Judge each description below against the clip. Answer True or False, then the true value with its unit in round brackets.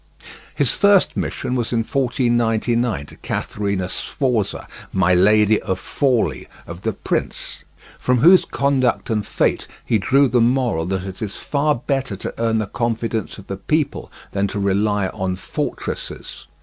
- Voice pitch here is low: True (115 Hz)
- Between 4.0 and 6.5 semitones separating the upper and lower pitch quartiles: True (4.4 semitones)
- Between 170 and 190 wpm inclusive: False (150 wpm)